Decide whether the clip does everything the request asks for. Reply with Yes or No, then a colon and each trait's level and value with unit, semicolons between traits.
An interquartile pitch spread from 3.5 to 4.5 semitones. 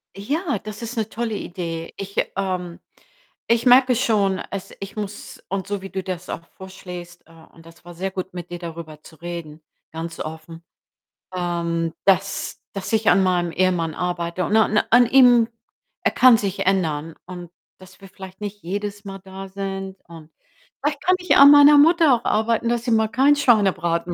Yes: average, 4.1 semitones